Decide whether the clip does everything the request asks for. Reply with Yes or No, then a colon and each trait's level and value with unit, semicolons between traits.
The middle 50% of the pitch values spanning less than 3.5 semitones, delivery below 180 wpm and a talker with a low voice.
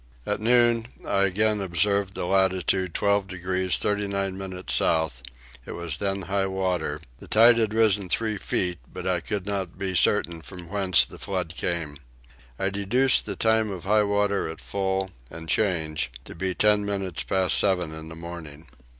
Yes: average, 2.8 semitones; average, 170 wpm; very low, 95 Hz